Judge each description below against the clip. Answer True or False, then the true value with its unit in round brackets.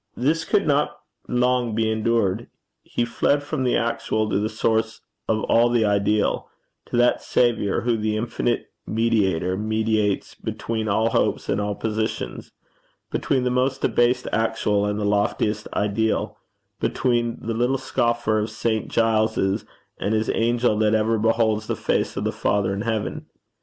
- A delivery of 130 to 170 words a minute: True (155 wpm)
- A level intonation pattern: True (1.9 semitones)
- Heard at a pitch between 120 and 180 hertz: False (110 Hz)